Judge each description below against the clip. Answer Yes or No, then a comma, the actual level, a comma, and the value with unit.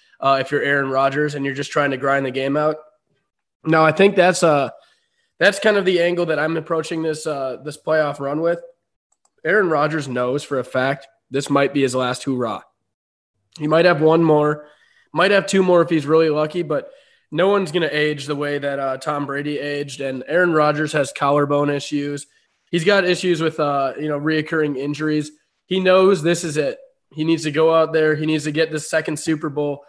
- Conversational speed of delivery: No, fast, 210 wpm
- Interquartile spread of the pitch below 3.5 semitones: Yes, narrow, 2.6 semitones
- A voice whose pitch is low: No, medium, 155 Hz